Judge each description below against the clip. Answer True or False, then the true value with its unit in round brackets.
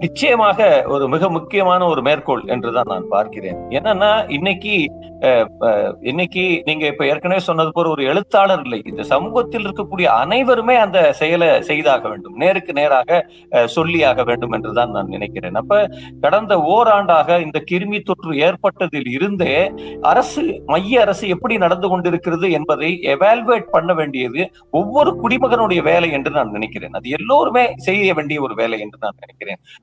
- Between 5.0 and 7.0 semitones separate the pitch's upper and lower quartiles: True (5.4 semitones)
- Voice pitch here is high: False (175 Hz)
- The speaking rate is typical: False (135 wpm)